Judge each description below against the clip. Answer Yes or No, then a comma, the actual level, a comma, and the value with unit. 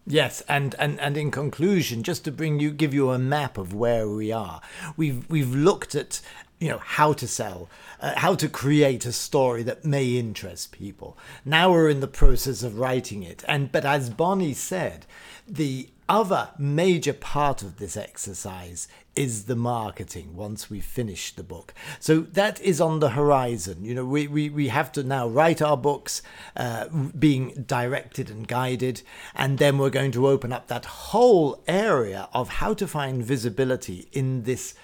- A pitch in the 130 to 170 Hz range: Yes, low, 135 Hz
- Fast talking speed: No, average, 180 wpm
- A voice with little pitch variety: No, average, 3.8 semitones